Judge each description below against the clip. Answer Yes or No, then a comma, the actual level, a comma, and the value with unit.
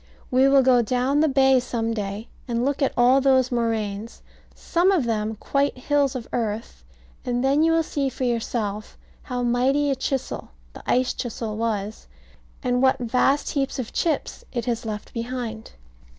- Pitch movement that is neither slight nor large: Yes, average, 3.0 semitones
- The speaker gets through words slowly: No, average, 165 wpm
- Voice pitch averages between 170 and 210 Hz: No, very high, 250 Hz